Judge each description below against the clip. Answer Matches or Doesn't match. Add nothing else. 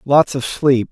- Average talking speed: Matches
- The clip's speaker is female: Doesn't match